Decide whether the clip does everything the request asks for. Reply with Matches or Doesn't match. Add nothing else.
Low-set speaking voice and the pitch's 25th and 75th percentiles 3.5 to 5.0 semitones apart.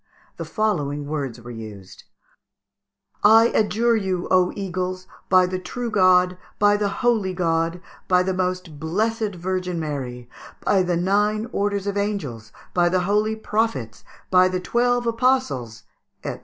Doesn't match